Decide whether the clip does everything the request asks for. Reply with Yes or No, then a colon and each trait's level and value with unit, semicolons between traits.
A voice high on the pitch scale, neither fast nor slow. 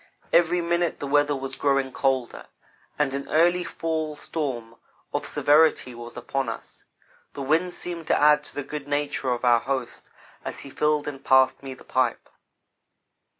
No: medium, 145 Hz; average, 165 wpm